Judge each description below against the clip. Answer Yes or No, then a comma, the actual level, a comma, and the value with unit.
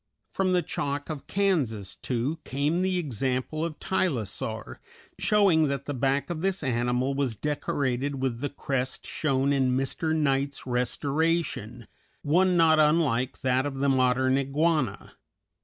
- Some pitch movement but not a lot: Yes, average, 3.6 semitones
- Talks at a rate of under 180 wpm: Yes, average, 140 wpm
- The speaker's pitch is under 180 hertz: Yes, medium, 140 Hz